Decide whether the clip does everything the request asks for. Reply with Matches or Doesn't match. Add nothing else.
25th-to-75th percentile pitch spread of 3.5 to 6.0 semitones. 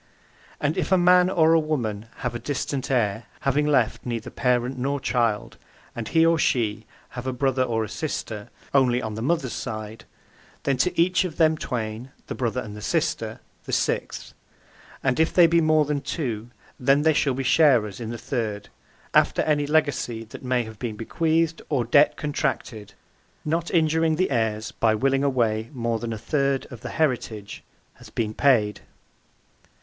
Matches